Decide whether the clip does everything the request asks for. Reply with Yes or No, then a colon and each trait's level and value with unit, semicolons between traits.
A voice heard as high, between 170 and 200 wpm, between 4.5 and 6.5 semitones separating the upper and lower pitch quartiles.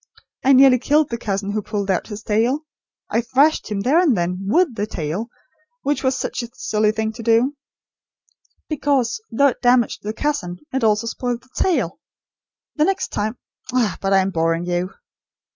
Yes: high, 230 Hz; average, 180 wpm; average, 4.8 semitones